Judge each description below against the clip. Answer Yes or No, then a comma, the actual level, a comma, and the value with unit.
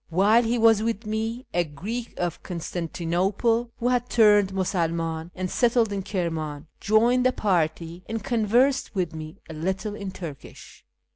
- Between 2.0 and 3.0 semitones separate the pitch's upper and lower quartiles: No, average, 5.1 semitones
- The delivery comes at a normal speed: Yes, average, 150 wpm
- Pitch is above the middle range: Yes, high, 195 Hz